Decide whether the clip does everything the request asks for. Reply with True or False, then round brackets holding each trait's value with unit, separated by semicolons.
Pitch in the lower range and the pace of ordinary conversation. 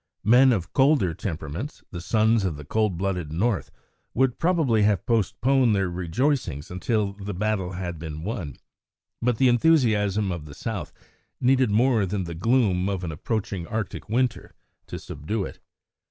True (105 Hz; 155 wpm)